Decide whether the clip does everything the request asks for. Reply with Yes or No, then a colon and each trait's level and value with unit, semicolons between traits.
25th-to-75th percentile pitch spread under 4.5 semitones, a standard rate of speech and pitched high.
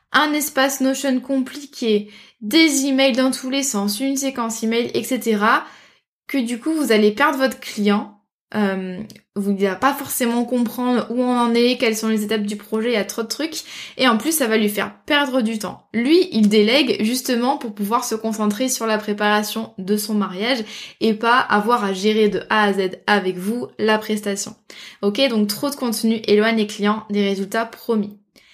Yes: average, 3.7 semitones; average, 195 wpm; high, 225 Hz